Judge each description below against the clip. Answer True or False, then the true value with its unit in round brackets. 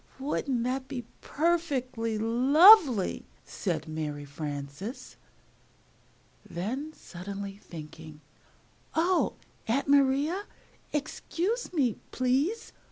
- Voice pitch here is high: True (255 Hz)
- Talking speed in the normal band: False (85 wpm)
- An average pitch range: False (8.4 semitones)